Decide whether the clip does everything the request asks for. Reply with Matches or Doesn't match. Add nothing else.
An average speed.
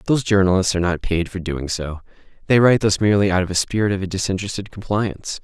Doesn't match